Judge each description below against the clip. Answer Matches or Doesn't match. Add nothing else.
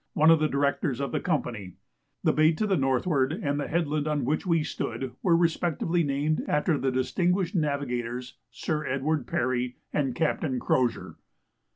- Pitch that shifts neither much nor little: Matches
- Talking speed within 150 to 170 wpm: Matches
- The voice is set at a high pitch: Doesn't match